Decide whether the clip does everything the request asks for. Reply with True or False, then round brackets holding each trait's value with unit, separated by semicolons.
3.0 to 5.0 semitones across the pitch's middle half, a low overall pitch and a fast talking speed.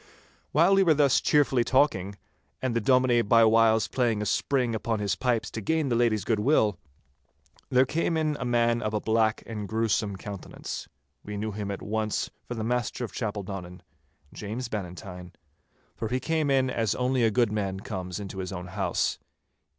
False (3.6 semitones; 115 Hz; 175 wpm)